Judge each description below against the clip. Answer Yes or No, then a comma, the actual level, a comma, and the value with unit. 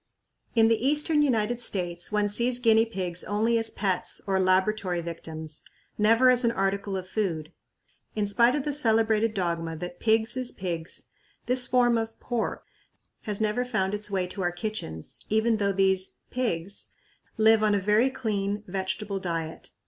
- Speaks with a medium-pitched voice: No, high, 210 Hz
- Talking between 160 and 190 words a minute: Yes, average, 165 wpm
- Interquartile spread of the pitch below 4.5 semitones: Yes, average, 3.4 semitones